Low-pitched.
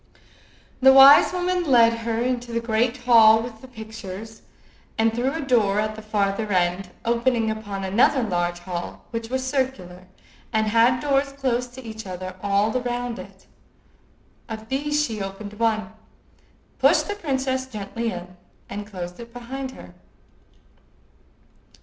No: high, 230 Hz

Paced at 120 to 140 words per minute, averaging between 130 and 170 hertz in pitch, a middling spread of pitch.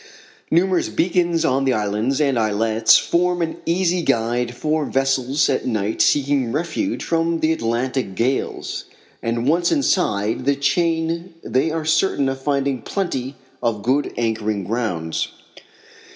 No: slow, 135 wpm; low, 135 Hz; wide, 6.0 semitones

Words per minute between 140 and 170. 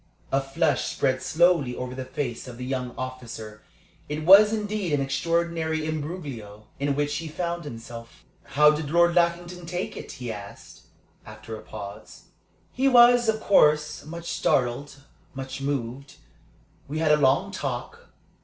Yes: average, 150 wpm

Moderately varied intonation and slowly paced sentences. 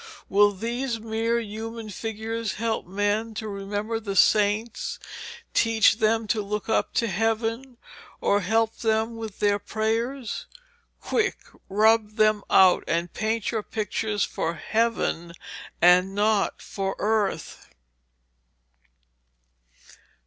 No: narrow, 1.8 semitones; slow, 115 wpm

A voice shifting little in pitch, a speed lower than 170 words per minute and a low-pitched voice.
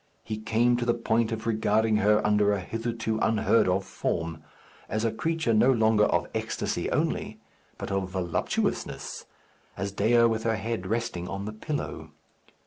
Yes: narrow, 2.1 semitones; average, 160 wpm; low, 110 Hz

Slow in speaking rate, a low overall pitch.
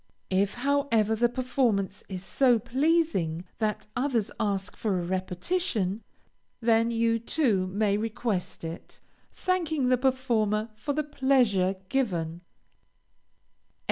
No: slow, 110 wpm; high, 225 Hz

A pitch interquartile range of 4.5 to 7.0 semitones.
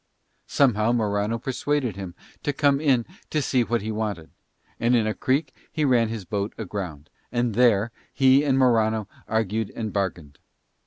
No: average, 3.9 semitones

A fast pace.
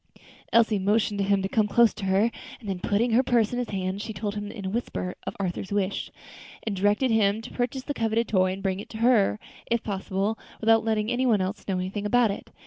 Yes: fast, 235 wpm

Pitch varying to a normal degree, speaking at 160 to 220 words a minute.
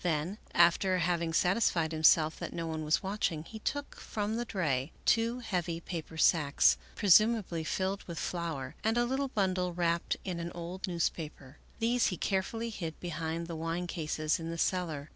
Yes: average, 3.3 semitones; average, 175 wpm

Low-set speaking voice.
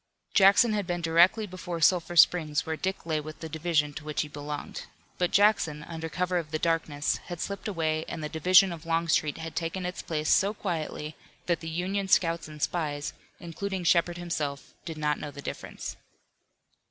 No: medium, 165 Hz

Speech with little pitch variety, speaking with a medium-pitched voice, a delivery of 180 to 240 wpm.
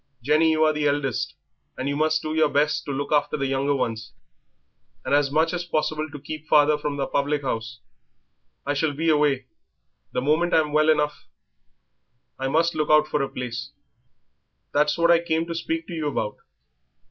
Yes: narrow, 2.0 semitones; medium, 150 Hz; average, 190 wpm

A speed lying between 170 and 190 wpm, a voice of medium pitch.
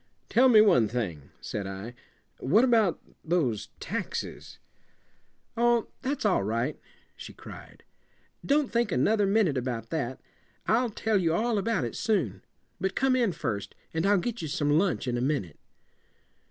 No: average, 155 wpm; medium, 175 Hz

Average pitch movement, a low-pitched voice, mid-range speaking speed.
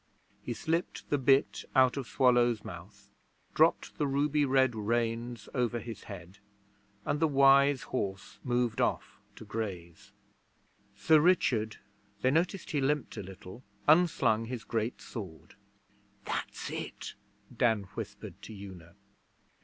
No: average, 4.6 semitones; low, 120 Hz; slow, 130 wpm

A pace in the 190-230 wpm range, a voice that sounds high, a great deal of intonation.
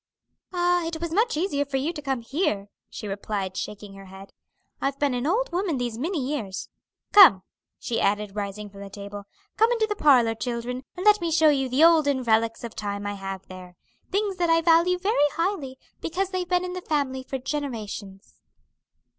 Yes: average, 195 wpm; very high, 270 Hz; wide, 8.6 semitones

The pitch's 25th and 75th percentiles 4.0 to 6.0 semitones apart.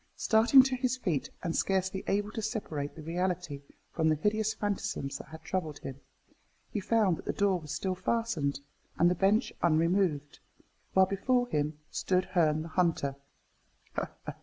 Yes: average, 4.9 semitones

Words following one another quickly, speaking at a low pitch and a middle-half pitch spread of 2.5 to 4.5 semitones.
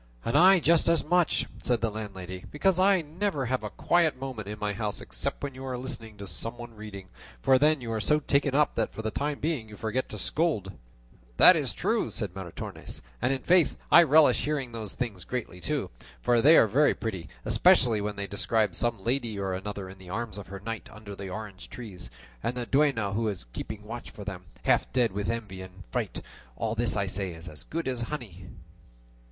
No: fast, 215 wpm; low, 115 Hz; average, 5.3 semitones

